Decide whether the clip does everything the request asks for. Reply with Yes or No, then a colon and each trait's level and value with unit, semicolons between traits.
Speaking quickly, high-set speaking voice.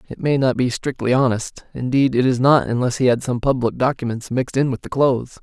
No: fast, 230 wpm; low, 125 Hz